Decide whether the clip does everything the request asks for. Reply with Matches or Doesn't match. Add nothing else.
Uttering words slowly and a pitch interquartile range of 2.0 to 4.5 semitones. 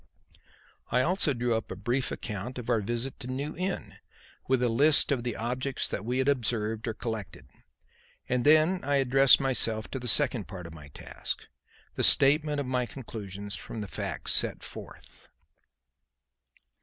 Doesn't match